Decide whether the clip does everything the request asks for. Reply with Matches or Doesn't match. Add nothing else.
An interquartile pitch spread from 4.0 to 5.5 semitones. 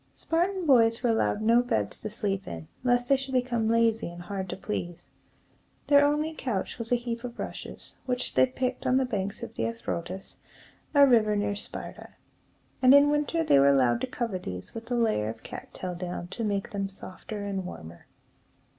Matches